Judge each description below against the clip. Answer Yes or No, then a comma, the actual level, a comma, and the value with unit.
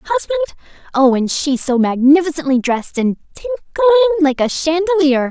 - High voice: Yes, very high, 315 Hz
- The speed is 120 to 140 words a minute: Yes, slow, 135 wpm